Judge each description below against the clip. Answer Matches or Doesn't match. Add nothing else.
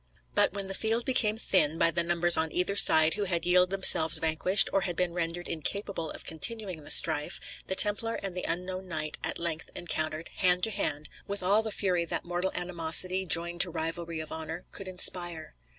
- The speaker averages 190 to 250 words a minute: Matches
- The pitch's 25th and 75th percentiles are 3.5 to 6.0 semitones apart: Doesn't match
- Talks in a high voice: Doesn't match